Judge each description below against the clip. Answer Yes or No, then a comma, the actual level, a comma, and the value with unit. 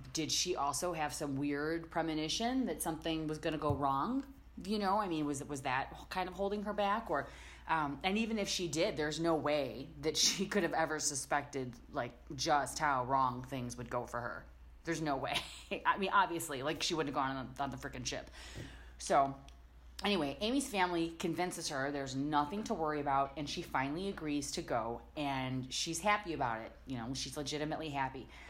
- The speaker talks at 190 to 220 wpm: Yes, average, 200 wpm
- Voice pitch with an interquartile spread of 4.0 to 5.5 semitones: Yes, average, 4.3 semitones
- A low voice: No, medium, 150 Hz